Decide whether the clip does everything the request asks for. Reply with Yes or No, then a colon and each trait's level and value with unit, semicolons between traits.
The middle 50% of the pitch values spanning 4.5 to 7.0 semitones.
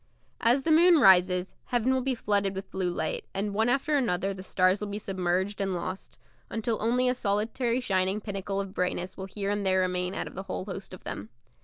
No: average, 3.7 semitones